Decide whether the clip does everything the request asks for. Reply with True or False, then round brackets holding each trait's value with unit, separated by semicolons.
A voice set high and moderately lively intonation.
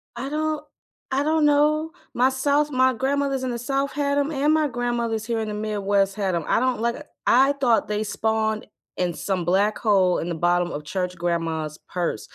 False (235 Hz; 6.3 semitones)